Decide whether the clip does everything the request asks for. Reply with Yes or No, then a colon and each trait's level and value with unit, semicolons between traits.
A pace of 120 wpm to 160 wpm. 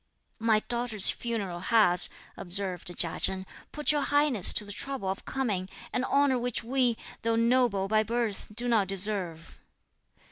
Yes: average, 150 wpm